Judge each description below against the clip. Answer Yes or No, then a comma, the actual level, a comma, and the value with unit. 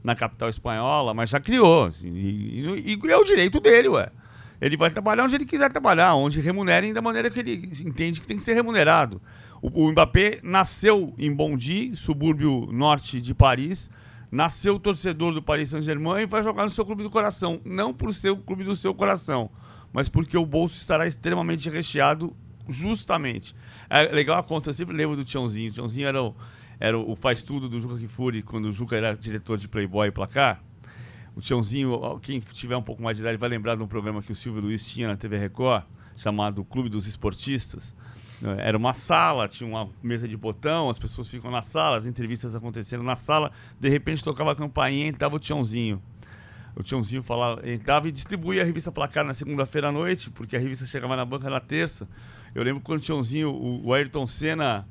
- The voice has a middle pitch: No, low, 130 Hz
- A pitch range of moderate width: No, wide, 5.9 semitones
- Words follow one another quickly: Yes, fast, 200 wpm